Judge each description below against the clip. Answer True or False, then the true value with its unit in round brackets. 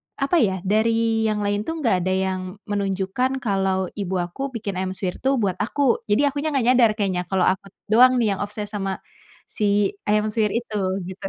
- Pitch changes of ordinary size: True (3.4 semitones)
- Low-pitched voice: False (205 Hz)